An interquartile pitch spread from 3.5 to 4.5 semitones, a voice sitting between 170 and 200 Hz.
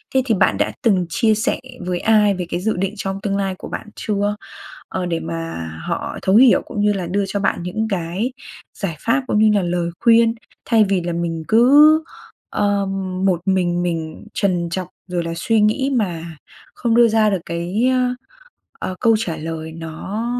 Yes: average, 4.2 semitones; high, 195 Hz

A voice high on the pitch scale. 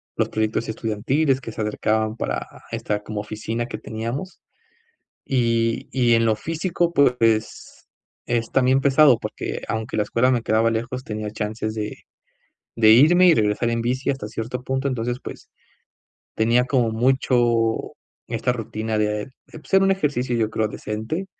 No: low, 115 Hz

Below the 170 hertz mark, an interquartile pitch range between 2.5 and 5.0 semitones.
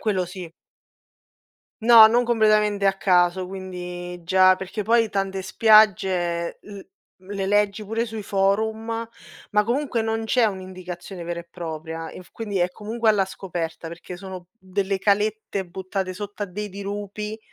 No: high, 195 Hz; average, 2.8 semitones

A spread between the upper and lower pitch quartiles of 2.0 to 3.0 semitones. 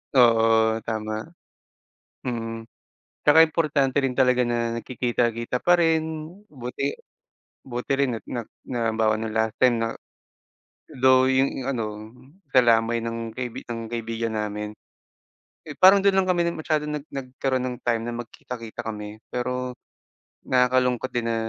Yes: narrow, 2.6 semitones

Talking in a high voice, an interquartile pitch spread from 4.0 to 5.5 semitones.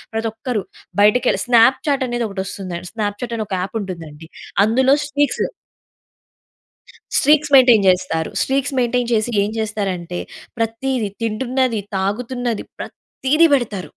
Yes: high, 230 Hz; average, 4.3 semitones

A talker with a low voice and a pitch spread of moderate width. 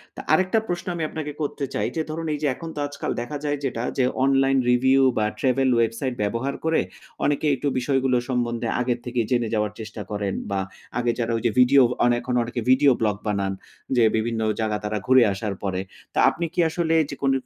Yes: low, 125 Hz; average, 3.8 semitones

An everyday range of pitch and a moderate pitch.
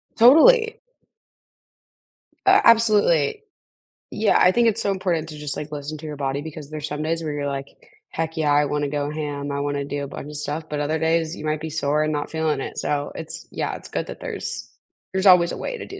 Yes: average, 3.2 semitones; medium, 155 Hz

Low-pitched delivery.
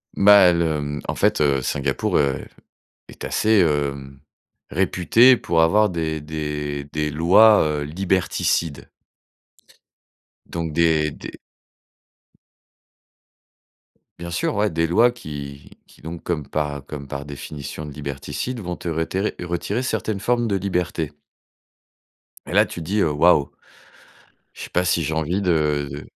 Yes: very low, 80 Hz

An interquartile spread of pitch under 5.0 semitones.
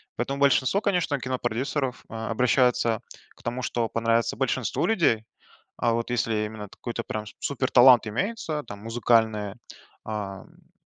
Yes: average, 2.7 semitones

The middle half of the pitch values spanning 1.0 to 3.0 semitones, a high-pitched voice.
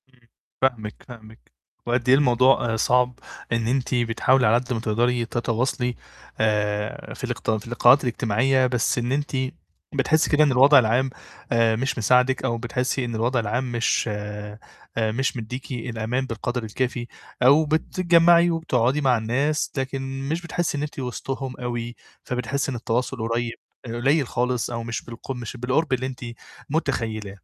No: narrow, 2.5 semitones; low, 125 Hz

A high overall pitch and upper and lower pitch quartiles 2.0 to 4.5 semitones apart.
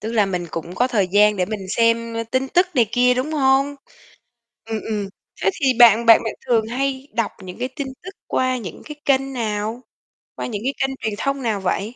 Yes: high, 230 Hz; average, 4.0 semitones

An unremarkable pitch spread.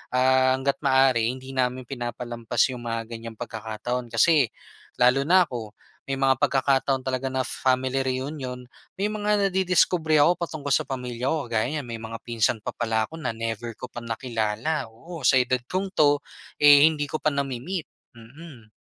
Yes: average, 3.7 semitones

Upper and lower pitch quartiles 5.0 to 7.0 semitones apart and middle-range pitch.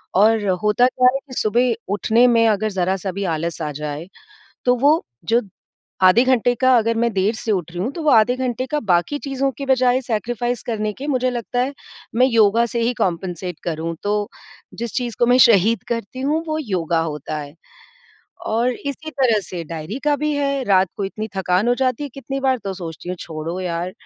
No: wide, 5.5 semitones; high, 230 Hz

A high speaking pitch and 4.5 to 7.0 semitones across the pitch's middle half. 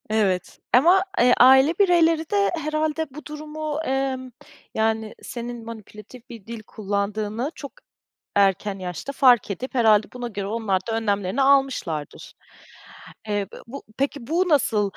Yes: high, 240 Hz; average, 5.2 semitones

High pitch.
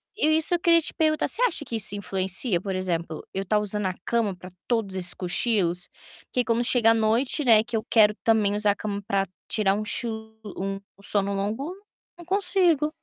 Yes: high, 215 Hz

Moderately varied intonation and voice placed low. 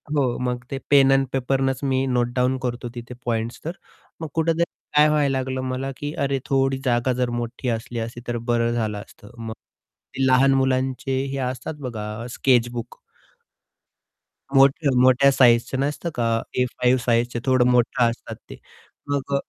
No: narrow, 2.1 semitones; low, 130 Hz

